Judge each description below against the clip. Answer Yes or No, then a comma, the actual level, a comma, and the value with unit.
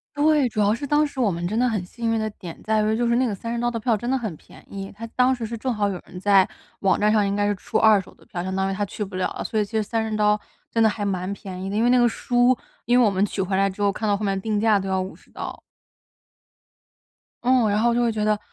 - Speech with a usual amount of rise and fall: Yes, average, 3.1 semitones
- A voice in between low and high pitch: No, high, 215 Hz